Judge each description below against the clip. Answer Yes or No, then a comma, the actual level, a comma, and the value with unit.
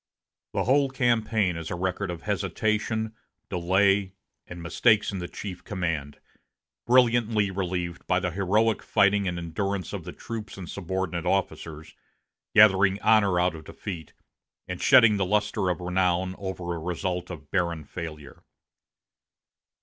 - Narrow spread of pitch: No, average, 3.1 semitones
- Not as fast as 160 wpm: Yes, average, 140 wpm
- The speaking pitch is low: Yes, very low, 95 Hz